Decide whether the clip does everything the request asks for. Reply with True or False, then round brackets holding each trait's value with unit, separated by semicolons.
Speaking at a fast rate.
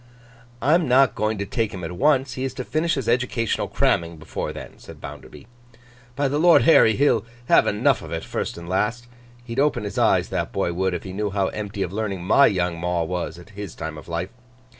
True (220 wpm)